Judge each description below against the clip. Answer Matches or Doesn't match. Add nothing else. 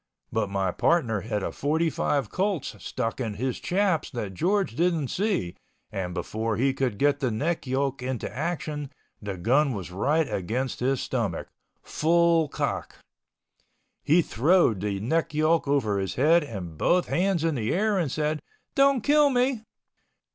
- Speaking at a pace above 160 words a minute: Doesn't match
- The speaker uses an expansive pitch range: Matches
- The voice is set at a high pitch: Doesn't match